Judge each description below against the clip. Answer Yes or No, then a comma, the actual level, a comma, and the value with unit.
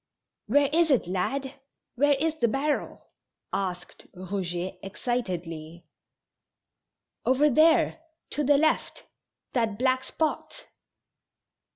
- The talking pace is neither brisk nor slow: No, slow, 95 wpm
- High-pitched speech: Yes, very high, 255 Hz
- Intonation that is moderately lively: No, wide, 7.6 semitones